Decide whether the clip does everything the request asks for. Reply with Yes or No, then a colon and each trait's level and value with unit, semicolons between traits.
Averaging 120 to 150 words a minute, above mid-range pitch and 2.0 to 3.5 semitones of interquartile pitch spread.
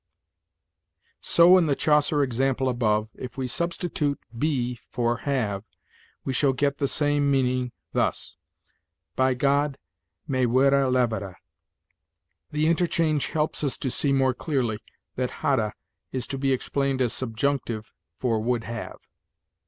No: slow, 135 wpm; low, 130 Hz; average, 2.8 semitones